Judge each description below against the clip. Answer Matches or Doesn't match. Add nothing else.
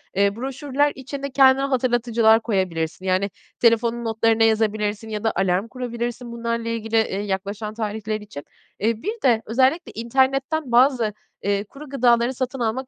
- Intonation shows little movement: Doesn't match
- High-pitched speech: Matches